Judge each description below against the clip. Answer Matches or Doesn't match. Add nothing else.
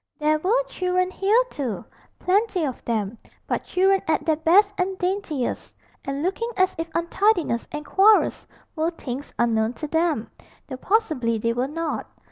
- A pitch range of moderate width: Doesn't match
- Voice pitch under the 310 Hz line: Doesn't match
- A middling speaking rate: Matches